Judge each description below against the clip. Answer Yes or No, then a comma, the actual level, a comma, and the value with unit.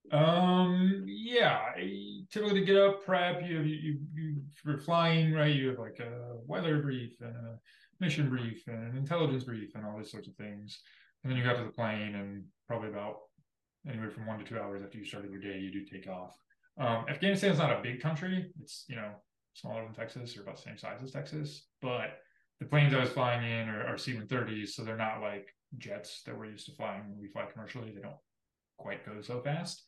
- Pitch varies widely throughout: Yes, wide, 6.1 semitones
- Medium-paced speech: No, fast, 225 wpm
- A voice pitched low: Yes, low, 125 Hz